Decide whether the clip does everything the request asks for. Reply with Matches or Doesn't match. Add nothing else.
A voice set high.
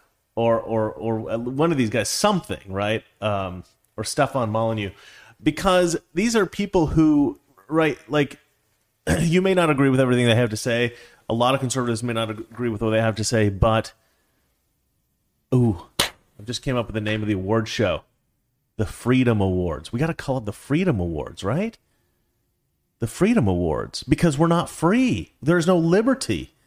Doesn't match